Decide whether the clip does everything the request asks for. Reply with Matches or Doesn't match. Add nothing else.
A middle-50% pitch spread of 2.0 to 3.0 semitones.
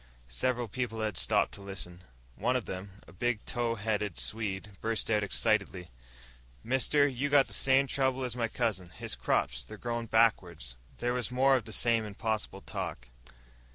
Doesn't match